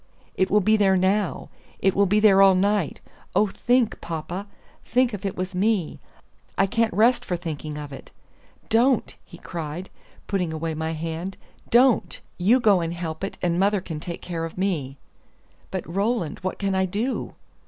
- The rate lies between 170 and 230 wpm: Yes, average, 180 wpm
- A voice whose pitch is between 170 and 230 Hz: Yes, high, 190 Hz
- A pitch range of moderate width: Yes, average, 3.7 semitones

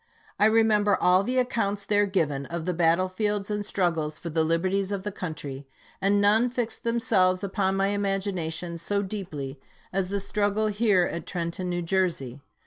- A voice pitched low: No, high, 190 Hz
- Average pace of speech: Yes, average, 170 wpm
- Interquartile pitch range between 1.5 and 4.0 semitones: Yes, average, 3.4 semitones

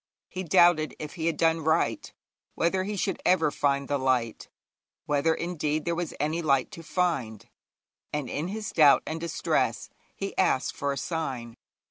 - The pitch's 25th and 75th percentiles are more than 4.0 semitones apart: No, average, 3.5 semitones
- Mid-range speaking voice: Yes, medium, 160 Hz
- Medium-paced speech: Yes, average, 165 wpm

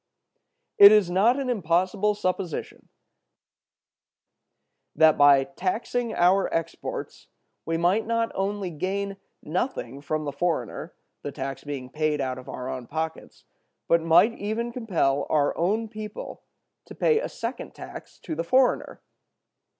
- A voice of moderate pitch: Yes, medium, 175 Hz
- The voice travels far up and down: Yes, wide, 5.7 semitones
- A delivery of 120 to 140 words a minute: Yes, slow, 135 wpm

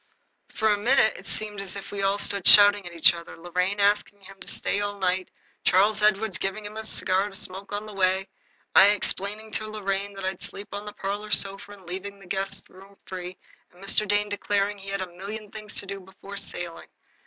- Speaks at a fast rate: Yes, fast, 215 wpm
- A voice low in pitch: No, high, 200 Hz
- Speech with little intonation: Yes, narrow, 1.4 semitones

